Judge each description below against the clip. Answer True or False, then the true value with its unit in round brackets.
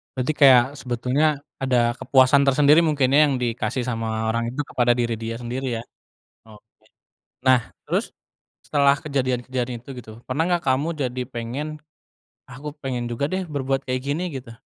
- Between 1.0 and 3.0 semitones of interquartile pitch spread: True (2.7 semitones)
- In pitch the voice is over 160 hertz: False (130 Hz)